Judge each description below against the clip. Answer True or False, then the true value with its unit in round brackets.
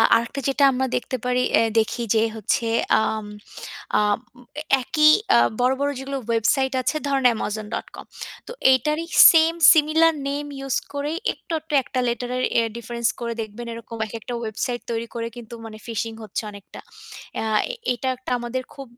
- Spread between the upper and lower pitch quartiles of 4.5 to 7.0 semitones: False (3.4 semitones)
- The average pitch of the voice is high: True (245 Hz)